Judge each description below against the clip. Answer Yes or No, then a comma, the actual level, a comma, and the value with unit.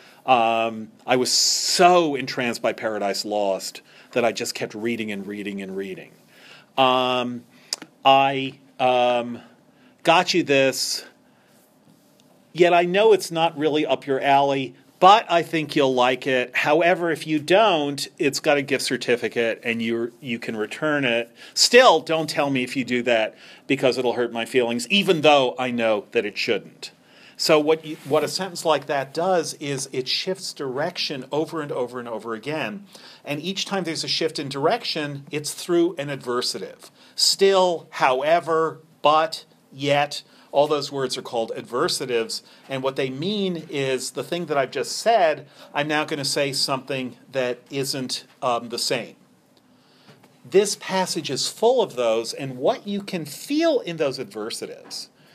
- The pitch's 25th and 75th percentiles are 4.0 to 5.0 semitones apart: Yes, average, 4.4 semitones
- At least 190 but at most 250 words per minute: No, average, 165 wpm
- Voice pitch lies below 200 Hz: Yes, medium, 140 Hz